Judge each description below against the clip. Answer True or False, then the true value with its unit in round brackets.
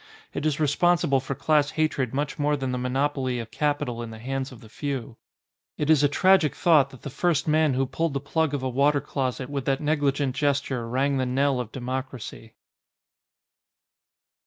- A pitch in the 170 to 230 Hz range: False (140 Hz)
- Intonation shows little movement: True (2.3 semitones)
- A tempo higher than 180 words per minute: True (190 wpm)